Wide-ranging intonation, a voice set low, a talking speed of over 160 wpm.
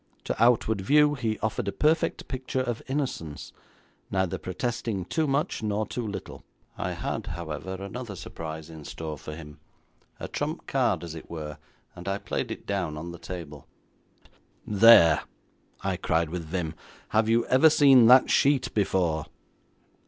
No: wide, 6.7 semitones; very low, 95 Hz; average, 155 wpm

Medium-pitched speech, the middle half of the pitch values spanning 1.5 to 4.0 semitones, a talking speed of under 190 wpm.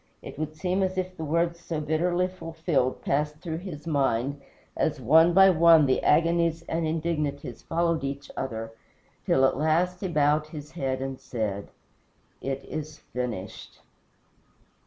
Yes: medium, 155 Hz; average, 3.5 semitones; average, 150 wpm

